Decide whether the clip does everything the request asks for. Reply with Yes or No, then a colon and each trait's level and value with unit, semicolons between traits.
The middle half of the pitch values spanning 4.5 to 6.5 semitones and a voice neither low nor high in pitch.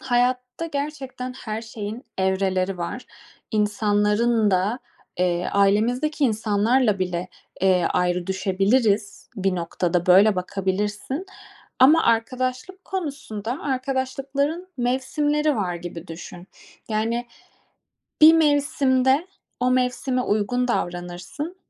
No: wide, 5.4 semitones; high, 225 Hz